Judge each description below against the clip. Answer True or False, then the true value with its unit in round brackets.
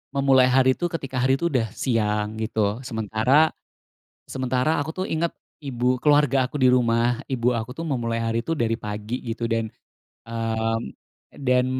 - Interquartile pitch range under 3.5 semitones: True (2.9 semitones)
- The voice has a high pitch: False (125 Hz)